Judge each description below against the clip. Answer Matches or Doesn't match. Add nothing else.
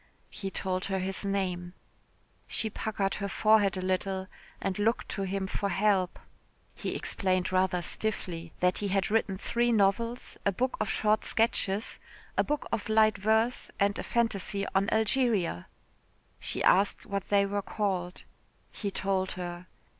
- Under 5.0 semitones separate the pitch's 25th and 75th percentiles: Matches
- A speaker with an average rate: Matches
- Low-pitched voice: Doesn't match